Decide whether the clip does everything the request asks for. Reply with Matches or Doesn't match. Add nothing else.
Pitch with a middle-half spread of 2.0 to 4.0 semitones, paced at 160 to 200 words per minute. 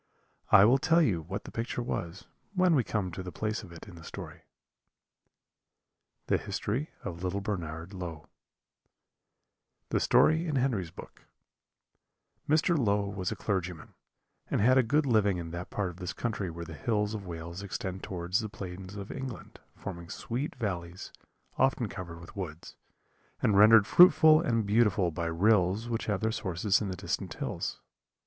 Doesn't match